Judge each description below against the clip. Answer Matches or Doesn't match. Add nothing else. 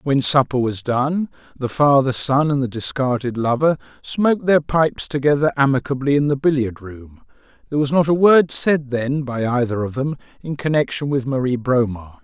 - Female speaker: Doesn't match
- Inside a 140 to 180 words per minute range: Matches